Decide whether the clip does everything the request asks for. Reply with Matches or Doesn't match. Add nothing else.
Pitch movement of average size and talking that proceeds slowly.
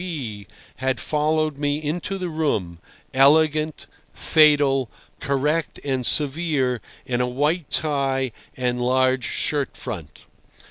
Matches